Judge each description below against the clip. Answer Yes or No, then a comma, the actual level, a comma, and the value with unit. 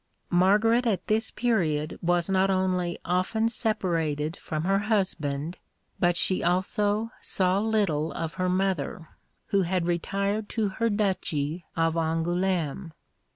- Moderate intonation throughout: Yes, average, 3.7 semitones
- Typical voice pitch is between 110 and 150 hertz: No, medium, 185 Hz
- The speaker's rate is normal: No, slow, 125 wpm